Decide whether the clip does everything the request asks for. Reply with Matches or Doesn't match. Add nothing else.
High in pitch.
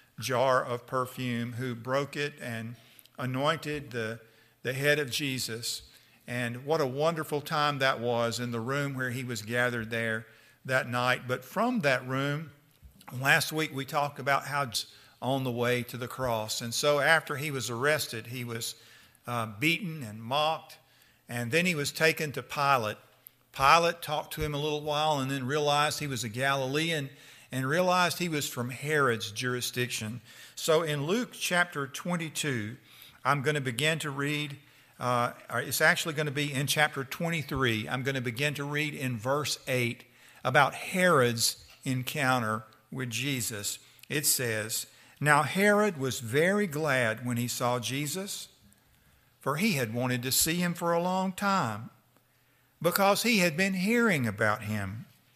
Doesn't match